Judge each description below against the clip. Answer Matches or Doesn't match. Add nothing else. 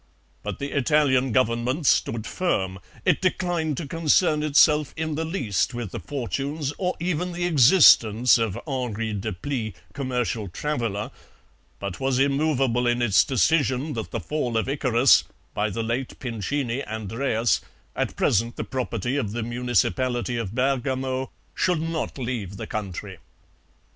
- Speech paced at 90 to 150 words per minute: Matches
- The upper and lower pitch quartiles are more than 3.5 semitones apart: Matches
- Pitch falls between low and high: Doesn't match